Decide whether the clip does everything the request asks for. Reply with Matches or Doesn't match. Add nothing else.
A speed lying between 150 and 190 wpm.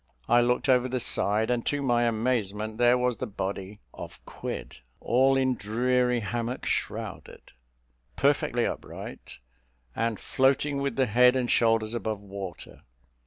Doesn't match